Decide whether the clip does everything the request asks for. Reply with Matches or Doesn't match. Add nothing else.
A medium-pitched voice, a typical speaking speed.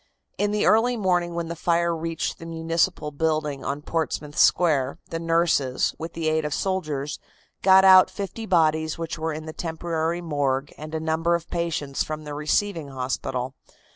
Matches